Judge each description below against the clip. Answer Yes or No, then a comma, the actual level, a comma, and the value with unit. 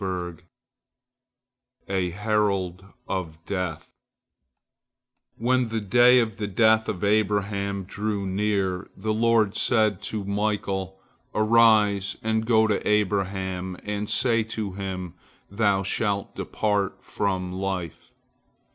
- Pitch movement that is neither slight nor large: No, narrow, 2.3 semitones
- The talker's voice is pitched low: Yes, low, 100 Hz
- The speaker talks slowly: Yes, slow, 105 wpm